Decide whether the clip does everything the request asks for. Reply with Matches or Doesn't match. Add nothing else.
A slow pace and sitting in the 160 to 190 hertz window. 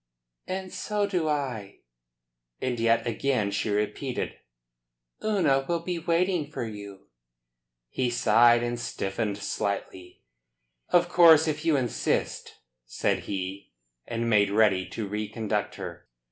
Doesn't match